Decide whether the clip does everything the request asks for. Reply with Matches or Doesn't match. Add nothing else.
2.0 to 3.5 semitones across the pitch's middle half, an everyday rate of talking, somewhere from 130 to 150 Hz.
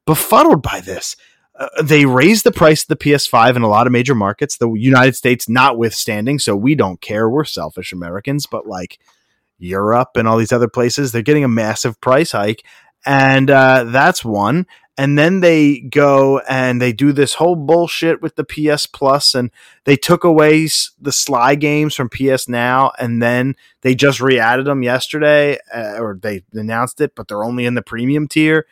Doesn't match